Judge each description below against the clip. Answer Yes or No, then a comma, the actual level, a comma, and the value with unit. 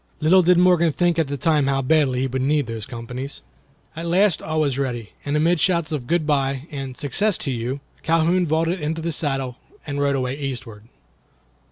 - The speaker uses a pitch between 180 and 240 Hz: No, medium, 145 Hz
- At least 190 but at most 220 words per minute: Yes, average, 195 wpm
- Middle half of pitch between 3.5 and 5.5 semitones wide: Yes, average, 3.8 semitones